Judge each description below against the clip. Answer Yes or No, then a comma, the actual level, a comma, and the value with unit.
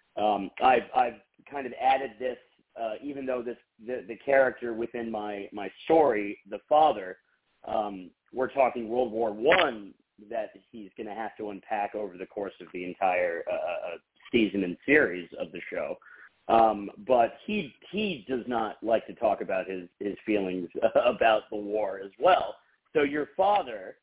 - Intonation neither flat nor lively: Yes, average, 4.5 semitones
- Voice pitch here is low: Yes, low, 115 Hz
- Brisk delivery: No, average, 165 wpm